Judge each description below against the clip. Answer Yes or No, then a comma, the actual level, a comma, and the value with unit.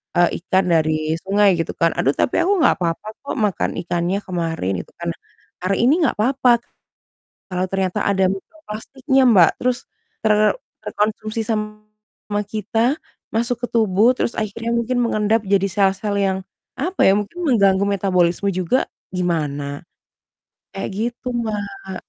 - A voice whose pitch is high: Yes, high, 205 Hz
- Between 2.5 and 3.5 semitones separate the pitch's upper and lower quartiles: No, average, 4.1 semitones